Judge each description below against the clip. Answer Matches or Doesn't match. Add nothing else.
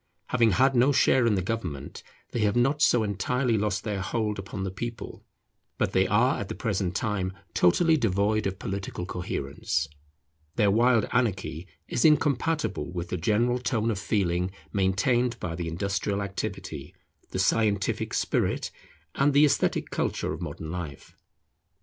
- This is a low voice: Matches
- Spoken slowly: Doesn't match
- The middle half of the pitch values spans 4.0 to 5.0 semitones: Matches